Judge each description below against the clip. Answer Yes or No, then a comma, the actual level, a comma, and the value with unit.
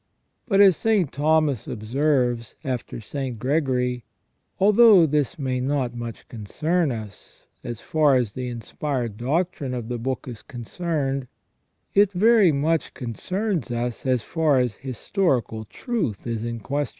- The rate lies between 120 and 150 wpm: Yes, average, 140 wpm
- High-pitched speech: No, low, 135 Hz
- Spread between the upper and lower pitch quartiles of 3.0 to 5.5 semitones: Yes, average, 5.1 semitones